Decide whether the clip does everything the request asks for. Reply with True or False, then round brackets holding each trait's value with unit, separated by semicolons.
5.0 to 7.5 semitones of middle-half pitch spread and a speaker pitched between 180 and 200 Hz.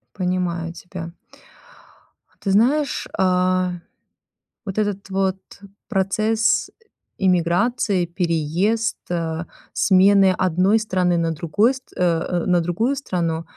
False (3.1 semitones; 185 Hz)